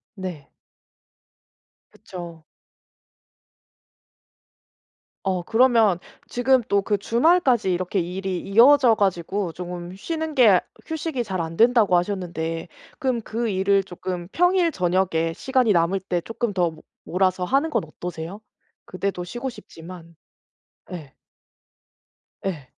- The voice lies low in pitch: No, high, 190 Hz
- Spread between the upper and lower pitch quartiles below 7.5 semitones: Yes, average, 5.3 semitones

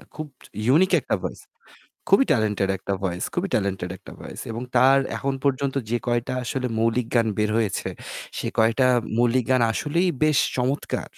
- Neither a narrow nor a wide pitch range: Yes, average, 3.6 semitones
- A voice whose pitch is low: Yes, low, 120 Hz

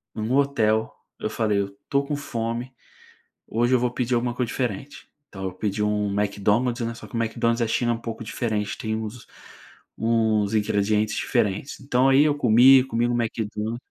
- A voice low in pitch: Yes, low, 115 Hz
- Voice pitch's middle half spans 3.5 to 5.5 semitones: No, narrow, 2.5 semitones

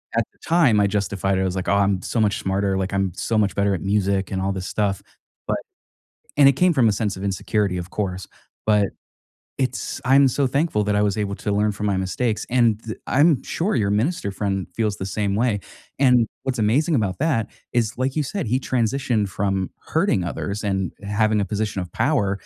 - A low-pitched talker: Yes, low, 105 Hz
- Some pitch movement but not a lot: Yes, average, 3.9 semitones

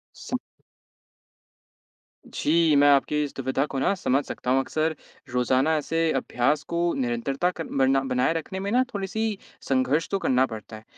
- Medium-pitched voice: Yes, medium, 145 Hz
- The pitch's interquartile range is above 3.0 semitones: Yes, average, 4.0 semitones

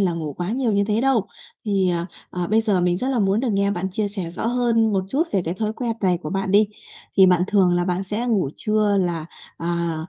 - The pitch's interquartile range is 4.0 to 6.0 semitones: No, average, 3.4 semitones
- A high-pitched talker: Yes, high, 195 Hz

